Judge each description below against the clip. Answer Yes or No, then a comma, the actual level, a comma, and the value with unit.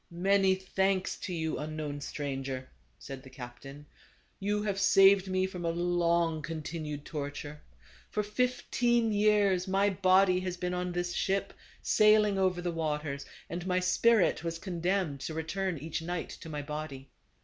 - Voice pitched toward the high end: No, medium, 175 Hz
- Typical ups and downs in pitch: Yes, average, 4.0 semitones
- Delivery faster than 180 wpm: No, average, 155 wpm